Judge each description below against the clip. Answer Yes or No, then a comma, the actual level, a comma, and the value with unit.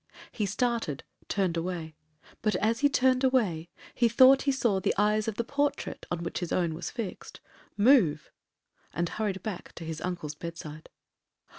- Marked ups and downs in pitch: Yes, wide, 5.8 semitones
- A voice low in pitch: No, high, 200 Hz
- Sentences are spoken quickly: No, average, 165 wpm